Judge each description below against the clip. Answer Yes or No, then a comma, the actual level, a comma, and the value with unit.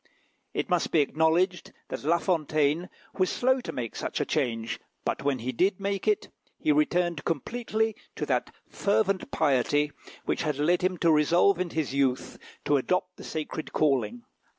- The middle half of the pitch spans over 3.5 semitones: Yes, average, 4.4 semitones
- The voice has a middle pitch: Yes, medium, 165 Hz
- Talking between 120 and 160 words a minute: No, average, 170 wpm